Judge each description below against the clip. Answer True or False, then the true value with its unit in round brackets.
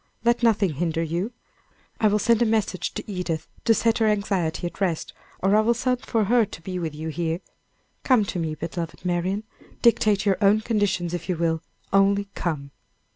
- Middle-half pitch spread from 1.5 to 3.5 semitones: False (4.3 semitones)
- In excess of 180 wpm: True (190 wpm)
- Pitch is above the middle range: True (195 Hz)